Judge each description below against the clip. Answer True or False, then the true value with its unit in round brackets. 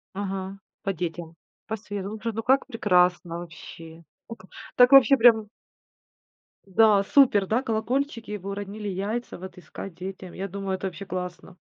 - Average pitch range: True (3.4 semitones)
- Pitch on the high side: True (195 Hz)